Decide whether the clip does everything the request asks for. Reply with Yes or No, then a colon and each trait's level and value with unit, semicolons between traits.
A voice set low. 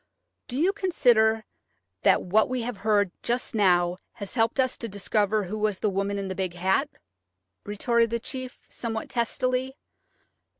No: high, 220 Hz